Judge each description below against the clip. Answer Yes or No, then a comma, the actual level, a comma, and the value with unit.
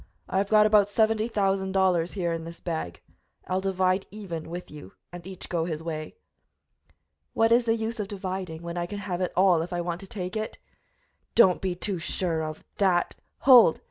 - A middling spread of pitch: Yes, average, 3.0 semitones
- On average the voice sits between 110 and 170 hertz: No, medium, 185 Hz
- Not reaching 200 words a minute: No, fast, 205 wpm